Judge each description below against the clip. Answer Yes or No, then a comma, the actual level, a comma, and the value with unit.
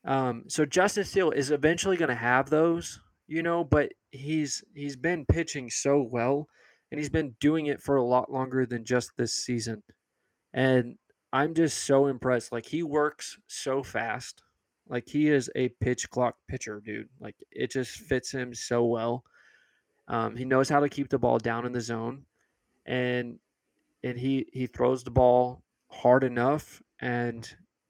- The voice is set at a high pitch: No, low, 130 Hz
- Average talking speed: Yes, average, 170 wpm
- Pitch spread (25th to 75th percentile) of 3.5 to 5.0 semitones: No, average, 3.1 semitones